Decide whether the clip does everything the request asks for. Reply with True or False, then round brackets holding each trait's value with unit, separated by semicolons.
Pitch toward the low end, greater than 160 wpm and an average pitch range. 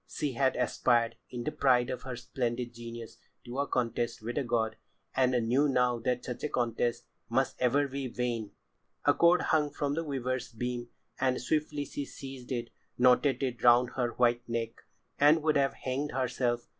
False (125 Hz; 180 wpm; 2.3 semitones)